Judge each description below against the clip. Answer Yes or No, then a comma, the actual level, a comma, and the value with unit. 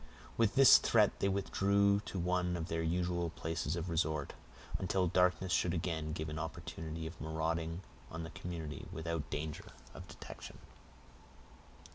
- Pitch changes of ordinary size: No, narrow, 2.1 semitones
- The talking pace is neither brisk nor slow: Yes, average, 150 wpm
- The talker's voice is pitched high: No, very low, 85 Hz